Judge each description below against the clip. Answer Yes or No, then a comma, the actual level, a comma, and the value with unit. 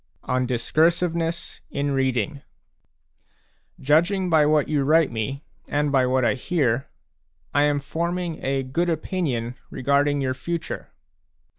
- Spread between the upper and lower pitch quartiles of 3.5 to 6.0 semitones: Yes, average, 3.9 semitones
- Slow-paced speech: Yes, slow, 125 wpm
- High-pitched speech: No, medium, 145 Hz